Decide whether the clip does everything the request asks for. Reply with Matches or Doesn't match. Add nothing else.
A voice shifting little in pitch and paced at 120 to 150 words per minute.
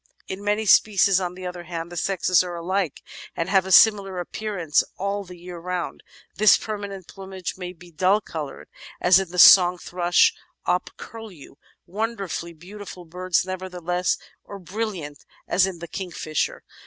Doesn't match